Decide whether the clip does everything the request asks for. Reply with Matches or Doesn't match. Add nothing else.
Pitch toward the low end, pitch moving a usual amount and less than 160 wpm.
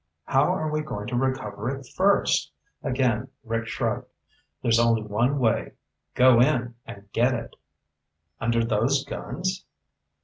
Matches